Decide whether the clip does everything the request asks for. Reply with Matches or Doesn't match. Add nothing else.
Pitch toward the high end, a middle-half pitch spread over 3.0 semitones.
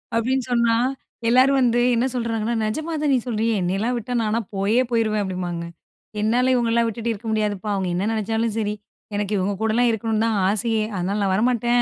Doesn't match